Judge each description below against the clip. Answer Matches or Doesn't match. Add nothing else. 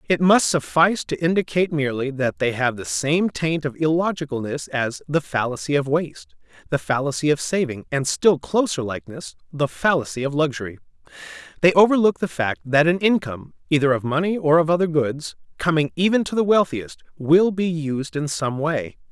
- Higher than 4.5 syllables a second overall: Matches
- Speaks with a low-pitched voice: Doesn't match